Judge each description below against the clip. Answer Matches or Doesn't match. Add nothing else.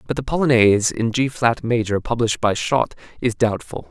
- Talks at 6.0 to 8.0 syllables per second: Doesn't match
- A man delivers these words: Matches